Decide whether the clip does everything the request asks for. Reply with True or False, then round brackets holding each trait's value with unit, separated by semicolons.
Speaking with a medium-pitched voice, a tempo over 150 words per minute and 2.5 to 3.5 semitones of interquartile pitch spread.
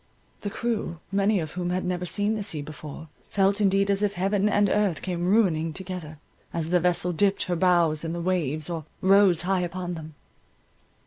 True (180 Hz; 190 wpm; 3.1 semitones)